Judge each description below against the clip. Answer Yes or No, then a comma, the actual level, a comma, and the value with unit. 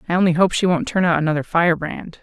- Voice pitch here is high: No, medium, 170 Hz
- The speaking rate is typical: No, fast, 245 wpm